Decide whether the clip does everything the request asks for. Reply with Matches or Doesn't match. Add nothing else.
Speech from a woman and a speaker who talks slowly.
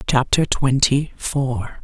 Matches